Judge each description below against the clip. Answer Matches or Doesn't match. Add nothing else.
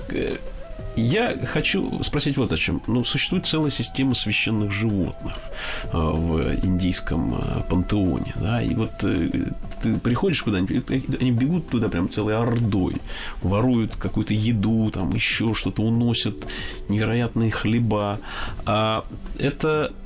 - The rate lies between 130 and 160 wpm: Doesn't match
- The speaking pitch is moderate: Doesn't match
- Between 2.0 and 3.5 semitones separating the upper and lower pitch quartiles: Doesn't match